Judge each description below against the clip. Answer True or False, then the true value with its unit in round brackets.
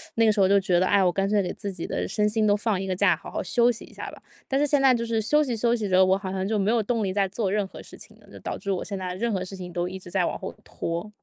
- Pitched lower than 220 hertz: True (200 Hz)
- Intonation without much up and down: False (3.1 semitones)